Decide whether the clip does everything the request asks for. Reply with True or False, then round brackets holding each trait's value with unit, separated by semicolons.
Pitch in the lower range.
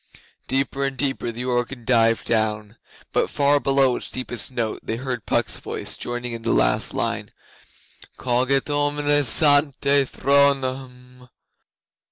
True (130 Hz)